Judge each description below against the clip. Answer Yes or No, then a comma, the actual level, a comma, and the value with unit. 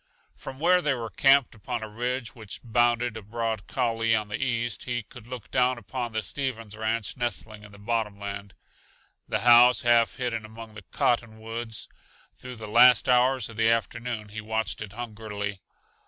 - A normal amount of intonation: No, narrow, 2.1 semitones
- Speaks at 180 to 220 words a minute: No, average, 170 wpm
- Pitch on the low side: Yes, low, 115 Hz